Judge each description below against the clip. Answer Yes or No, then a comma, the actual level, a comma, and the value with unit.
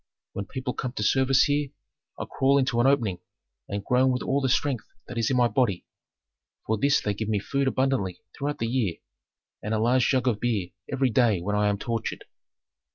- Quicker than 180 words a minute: Yes, fast, 205 wpm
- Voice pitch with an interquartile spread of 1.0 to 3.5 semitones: No, average, 4.0 semitones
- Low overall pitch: Yes, low, 120 Hz